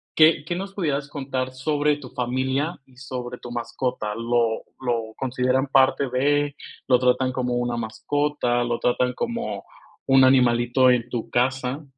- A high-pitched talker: No, low, 130 Hz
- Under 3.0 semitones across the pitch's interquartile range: Yes, narrow, 2.5 semitones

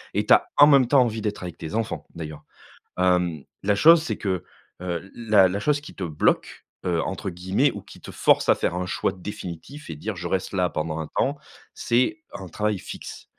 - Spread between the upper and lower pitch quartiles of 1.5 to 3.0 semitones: No, average, 4.5 semitones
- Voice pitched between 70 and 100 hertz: Yes, very low, 95 Hz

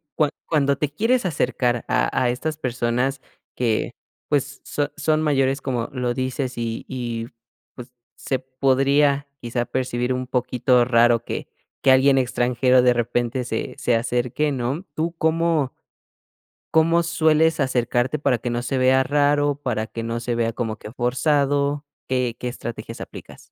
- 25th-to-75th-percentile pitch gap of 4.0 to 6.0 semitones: No, average, 3.0 semitones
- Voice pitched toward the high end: No, low, 130 Hz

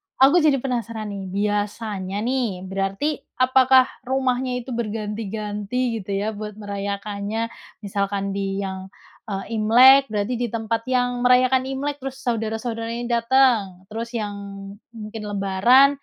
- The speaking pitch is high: Yes, high, 225 Hz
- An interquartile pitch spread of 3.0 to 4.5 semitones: Yes, average, 3.8 semitones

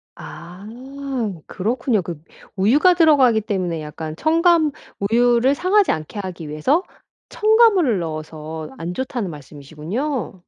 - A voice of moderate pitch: No, high, 205 Hz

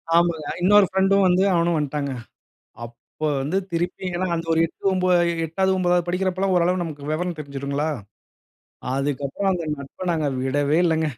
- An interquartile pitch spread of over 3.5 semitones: Yes, average, 3.9 semitones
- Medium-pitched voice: Yes, medium, 170 Hz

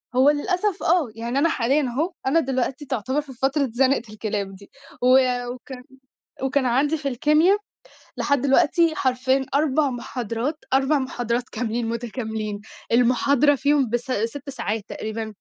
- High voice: Yes, very high, 260 Hz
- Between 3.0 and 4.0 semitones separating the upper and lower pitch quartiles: Yes, average, 3.5 semitones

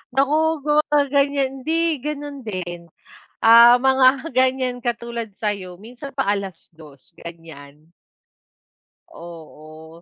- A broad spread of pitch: Yes, wide, 8.3 semitones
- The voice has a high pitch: Yes, high, 235 Hz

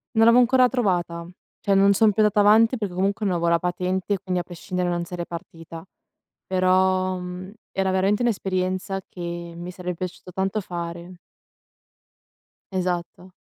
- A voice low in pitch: No, medium, 185 Hz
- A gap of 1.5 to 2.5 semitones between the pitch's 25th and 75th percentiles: Yes, narrow, 2.1 semitones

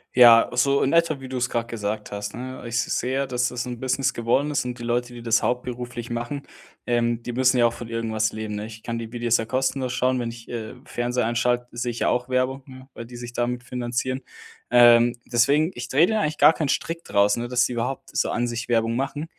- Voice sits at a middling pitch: No, low, 120 Hz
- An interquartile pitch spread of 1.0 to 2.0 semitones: Yes, narrow, 1.7 semitones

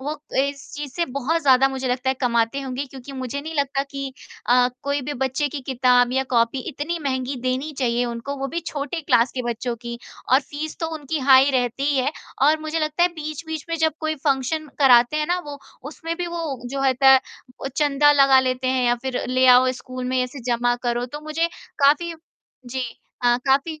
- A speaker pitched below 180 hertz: No, very high, 270 Hz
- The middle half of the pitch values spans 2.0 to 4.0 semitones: Yes, average, 2.8 semitones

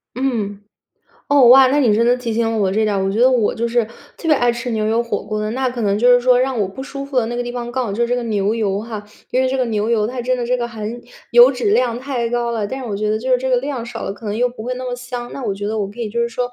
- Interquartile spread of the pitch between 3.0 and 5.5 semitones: No, narrow, 2.6 semitones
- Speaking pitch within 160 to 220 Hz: No, high, 235 Hz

